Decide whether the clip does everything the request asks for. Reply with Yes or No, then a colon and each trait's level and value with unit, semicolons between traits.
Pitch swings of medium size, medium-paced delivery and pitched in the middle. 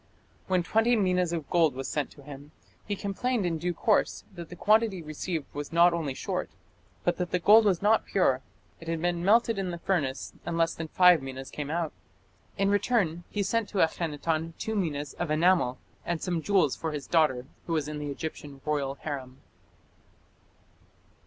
Yes: average, 4.1 semitones; average, 185 wpm; medium, 170 Hz